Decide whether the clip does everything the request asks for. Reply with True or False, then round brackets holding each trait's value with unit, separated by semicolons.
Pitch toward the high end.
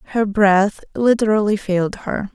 True (205 Hz)